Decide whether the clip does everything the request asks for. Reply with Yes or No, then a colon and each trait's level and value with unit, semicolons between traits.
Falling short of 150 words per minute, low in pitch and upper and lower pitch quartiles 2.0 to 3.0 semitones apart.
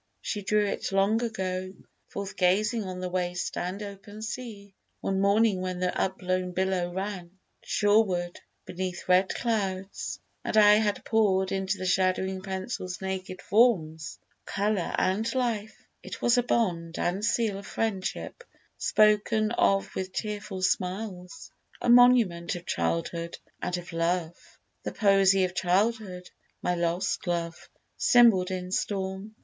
No: slow, 135 wpm; high, 190 Hz; narrow, 2.6 semitones